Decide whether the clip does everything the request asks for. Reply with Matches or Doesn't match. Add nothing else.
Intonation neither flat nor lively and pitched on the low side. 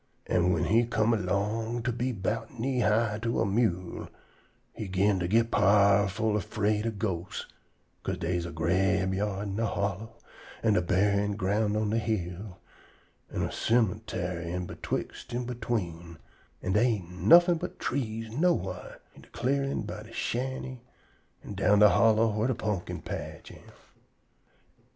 Matches